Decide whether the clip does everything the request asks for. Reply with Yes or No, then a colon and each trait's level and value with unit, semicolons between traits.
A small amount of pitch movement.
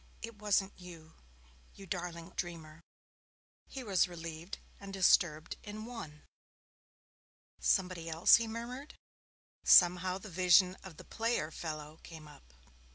No: average, 3.7 semitones